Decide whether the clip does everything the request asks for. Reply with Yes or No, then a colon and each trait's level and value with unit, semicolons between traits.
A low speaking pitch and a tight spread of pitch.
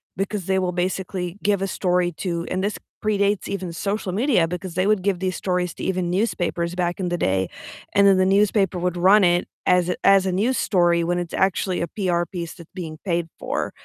No: medium, 185 Hz; narrow, 2.0 semitones